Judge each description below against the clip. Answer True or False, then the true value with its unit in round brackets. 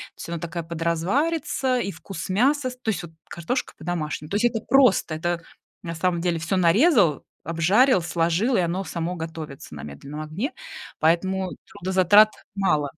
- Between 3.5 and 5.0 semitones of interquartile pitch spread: True (4.4 semitones)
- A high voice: False (175 Hz)